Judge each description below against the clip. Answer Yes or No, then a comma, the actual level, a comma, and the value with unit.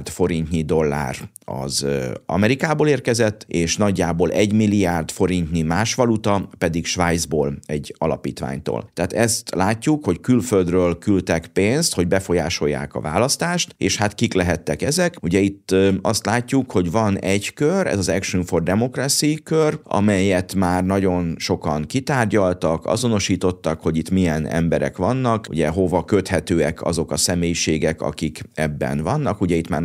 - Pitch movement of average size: Yes, average, 4.5 semitones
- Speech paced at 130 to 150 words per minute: Yes, average, 140 wpm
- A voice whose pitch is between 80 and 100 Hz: Yes, very low, 95 Hz